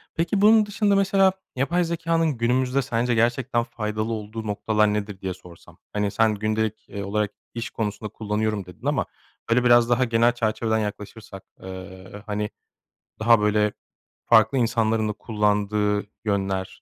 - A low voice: Yes, low, 110 Hz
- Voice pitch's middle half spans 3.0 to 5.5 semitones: No, narrow, 2.6 semitones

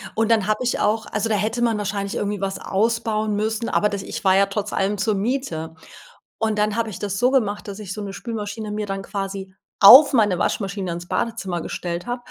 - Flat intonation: Yes, narrow, 2.3 semitones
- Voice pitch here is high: Yes, high, 210 Hz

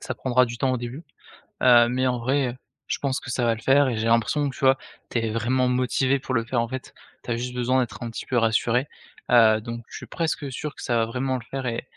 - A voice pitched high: No, low, 125 Hz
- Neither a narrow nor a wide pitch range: No, narrow, 2.0 semitones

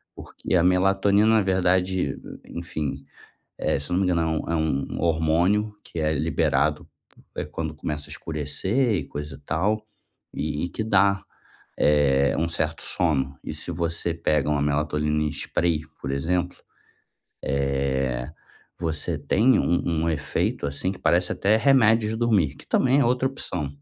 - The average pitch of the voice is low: Yes, very low, 80 Hz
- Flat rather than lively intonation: No, average, 4.5 semitones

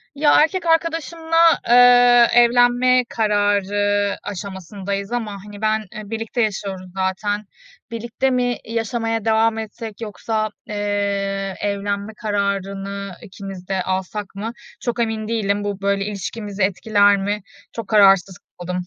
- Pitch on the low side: No, high, 205 Hz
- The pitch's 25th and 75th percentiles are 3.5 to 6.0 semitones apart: No, narrow, 2.5 semitones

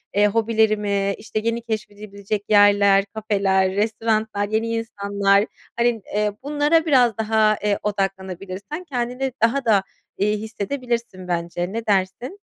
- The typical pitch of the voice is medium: No, high, 215 Hz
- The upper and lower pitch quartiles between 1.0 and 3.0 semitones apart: Yes, narrow, 2.4 semitones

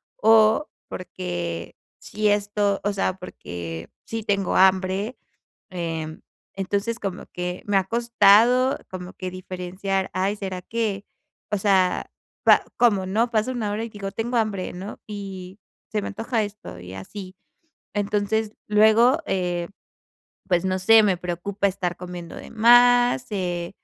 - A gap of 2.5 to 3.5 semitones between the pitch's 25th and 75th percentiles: Yes, average, 2.9 semitones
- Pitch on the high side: Yes, high, 200 Hz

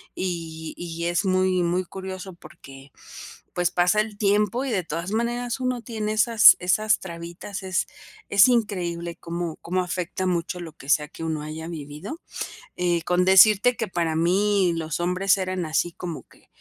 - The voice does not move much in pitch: No, average, 3.3 semitones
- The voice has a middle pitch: Yes, medium, 180 Hz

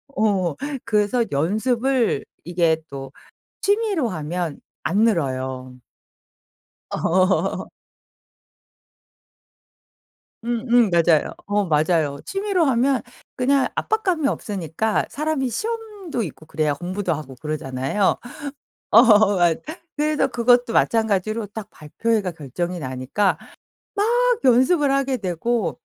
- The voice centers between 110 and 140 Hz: No, high, 205 Hz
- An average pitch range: No, wide, 7.7 semitones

